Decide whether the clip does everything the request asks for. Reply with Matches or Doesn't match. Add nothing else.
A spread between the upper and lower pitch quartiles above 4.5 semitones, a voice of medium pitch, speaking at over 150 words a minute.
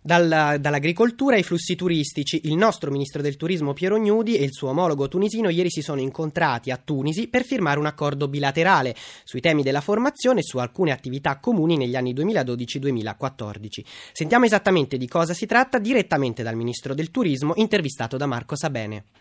Matches